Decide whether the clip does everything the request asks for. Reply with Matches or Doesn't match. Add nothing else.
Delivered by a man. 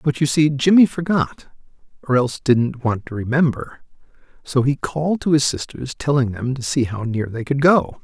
Matches